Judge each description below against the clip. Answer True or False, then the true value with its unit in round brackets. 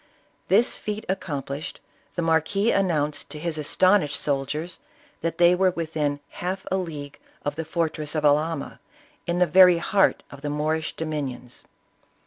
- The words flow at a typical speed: True (150 wpm)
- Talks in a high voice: False (160 Hz)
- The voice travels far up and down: False (3.4 semitones)